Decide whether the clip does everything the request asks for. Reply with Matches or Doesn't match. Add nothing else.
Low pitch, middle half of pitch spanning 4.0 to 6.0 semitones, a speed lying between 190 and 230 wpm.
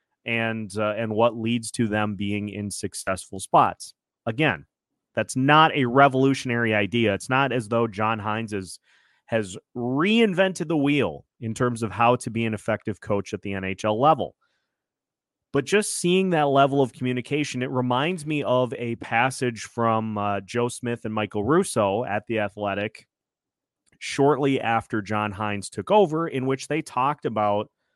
Doesn't match